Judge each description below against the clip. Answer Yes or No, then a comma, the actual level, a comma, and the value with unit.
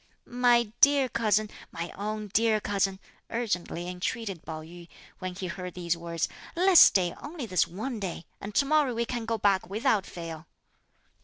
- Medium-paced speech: Yes, average, 165 wpm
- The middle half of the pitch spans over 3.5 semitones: Yes, average, 4.6 semitones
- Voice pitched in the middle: No, high, 200 Hz